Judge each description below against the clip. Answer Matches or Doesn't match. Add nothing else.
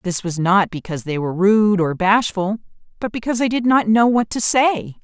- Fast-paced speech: Matches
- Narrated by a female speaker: Matches